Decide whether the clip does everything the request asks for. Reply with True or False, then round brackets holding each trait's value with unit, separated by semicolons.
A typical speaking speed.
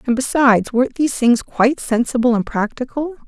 True (165 wpm)